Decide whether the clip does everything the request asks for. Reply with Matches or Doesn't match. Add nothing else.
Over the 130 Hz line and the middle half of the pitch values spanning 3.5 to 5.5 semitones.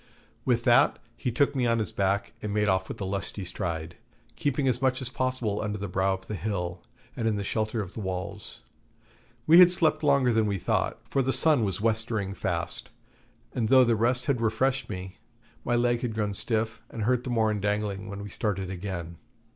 Doesn't match